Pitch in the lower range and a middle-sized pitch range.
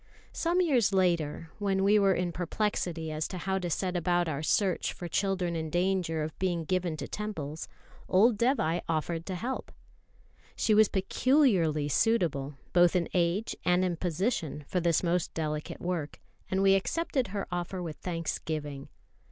No: medium, 180 Hz; average, 3.2 semitones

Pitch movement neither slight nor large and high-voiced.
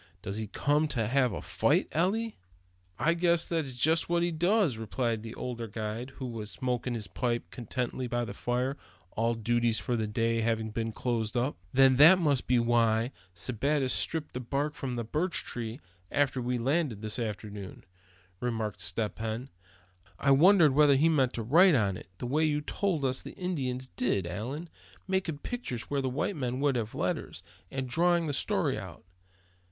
No: average, 4.6 semitones; low, 125 Hz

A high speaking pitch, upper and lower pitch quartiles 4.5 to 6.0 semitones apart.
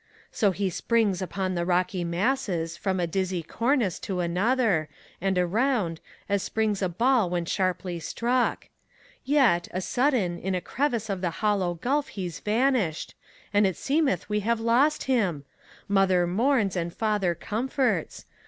Yes: high, 195 Hz; average, 4.8 semitones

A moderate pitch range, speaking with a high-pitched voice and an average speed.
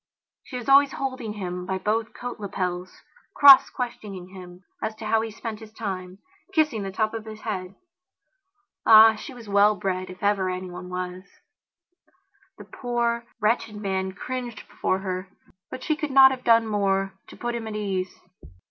Yes: average, 3.9 semitones; high, 210 Hz; average, 170 wpm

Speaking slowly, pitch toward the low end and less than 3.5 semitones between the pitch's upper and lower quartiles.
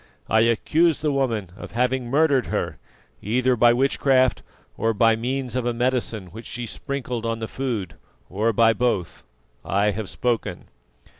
No: average, 155 wpm; low, 120 Hz; narrow, 2.5 semitones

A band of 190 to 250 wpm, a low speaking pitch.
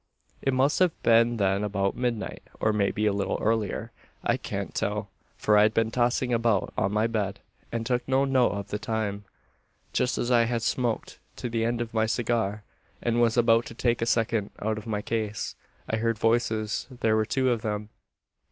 Yes: average, 195 wpm; low, 115 Hz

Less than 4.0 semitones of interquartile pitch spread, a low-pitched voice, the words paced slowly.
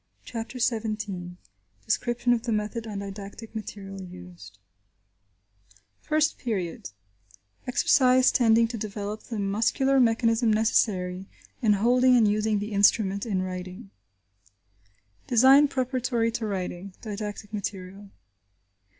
No: average, 3.2 semitones; high, 215 Hz; slow, 105 wpm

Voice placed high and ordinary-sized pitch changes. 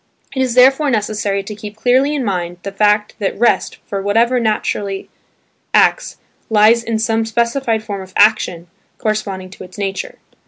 Yes: high, 215 Hz; average, 3.0 semitones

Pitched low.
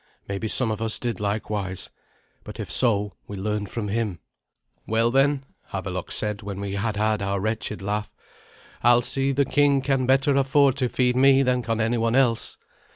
Yes: low, 115 Hz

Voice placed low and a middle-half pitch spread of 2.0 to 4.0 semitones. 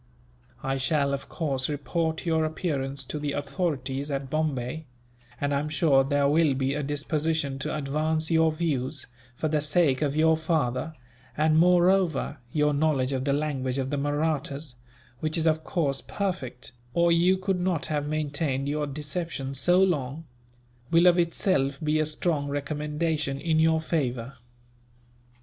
No: medium, 150 Hz; average, 2.7 semitones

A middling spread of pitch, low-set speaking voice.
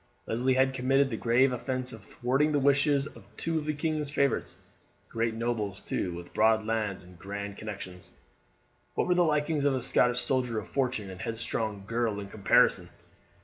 Yes: average, 4.3 semitones; low, 120 Hz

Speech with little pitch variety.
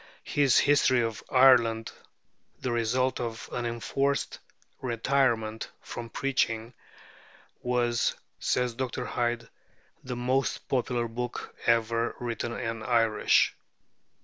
Yes: narrow, 1.8 semitones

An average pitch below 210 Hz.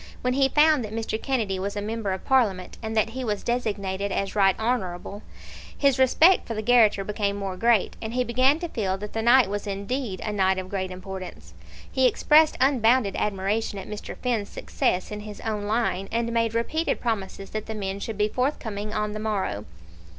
No: high, 215 Hz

